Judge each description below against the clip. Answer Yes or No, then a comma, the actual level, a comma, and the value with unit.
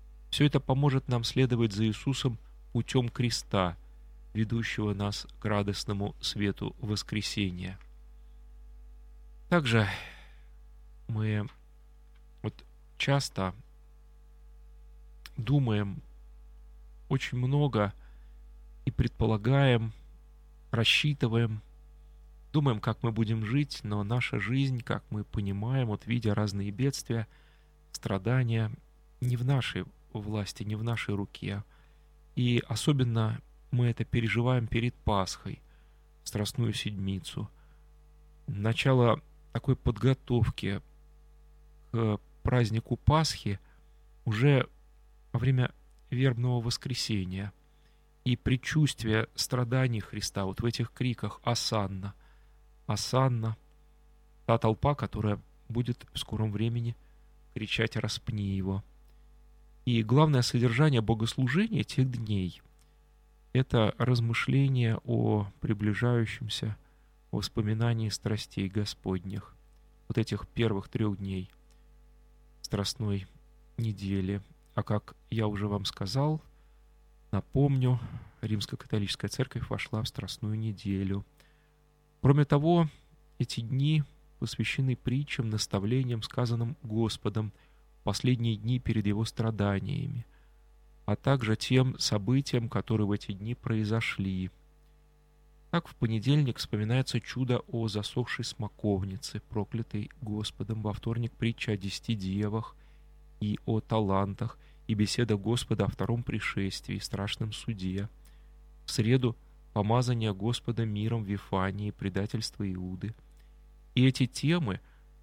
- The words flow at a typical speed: No, slow, 95 wpm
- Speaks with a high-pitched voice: No, low, 110 Hz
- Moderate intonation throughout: Yes, average, 4.2 semitones